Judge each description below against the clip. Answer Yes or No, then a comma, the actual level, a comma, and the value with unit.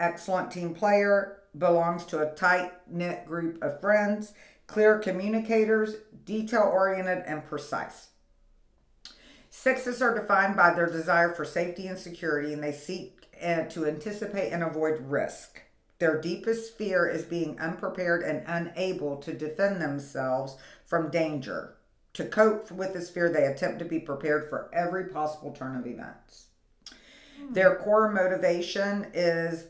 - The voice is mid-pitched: Yes, medium, 175 Hz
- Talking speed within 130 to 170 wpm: Yes, slow, 135 wpm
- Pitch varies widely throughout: No, average, 3.8 semitones